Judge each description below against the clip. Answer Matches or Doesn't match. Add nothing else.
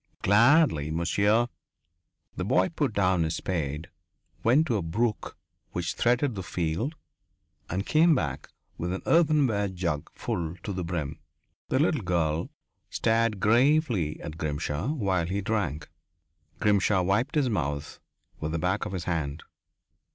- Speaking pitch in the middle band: Doesn't match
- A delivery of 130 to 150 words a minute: Matches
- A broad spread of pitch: Matches